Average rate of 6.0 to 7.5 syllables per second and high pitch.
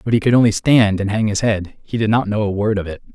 No: 6.2 syllables/s; low, 105 Hz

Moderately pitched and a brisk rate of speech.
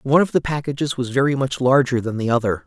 No: low, 130 Hz; fast, 250 wpm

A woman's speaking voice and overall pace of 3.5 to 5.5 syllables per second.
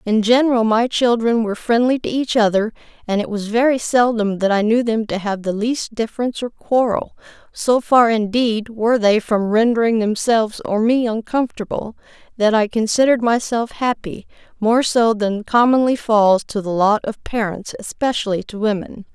Yes: female; 5.0 syllables/s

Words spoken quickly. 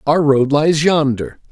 No: average, 160 wpm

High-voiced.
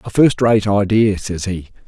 No: low, 100 Hz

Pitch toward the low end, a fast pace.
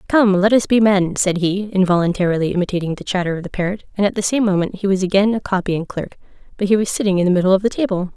No: high, 190 Hz; fast, 255 wpm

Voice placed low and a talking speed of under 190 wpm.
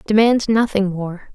No: high, 205 Hz; slow, 135 wpm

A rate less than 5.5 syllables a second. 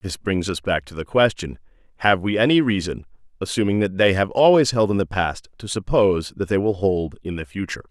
No: 5.6 syllables/s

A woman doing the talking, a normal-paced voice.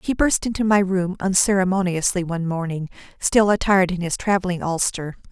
Yes: female; average, 160 wpm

